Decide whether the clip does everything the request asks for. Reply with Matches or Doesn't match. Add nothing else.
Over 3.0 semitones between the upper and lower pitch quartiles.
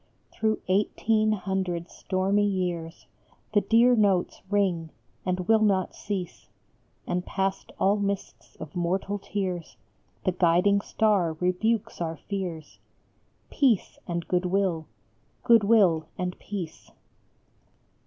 Doesn't match